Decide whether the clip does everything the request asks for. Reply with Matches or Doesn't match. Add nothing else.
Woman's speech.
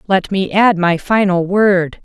Matches